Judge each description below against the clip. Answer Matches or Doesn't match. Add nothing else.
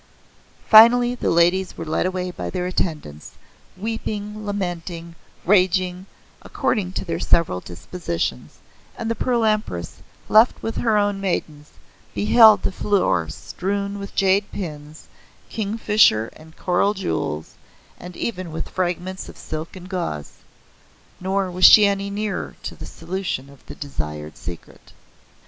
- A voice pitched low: Doesn't match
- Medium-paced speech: Doesn't match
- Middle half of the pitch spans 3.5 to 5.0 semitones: Matches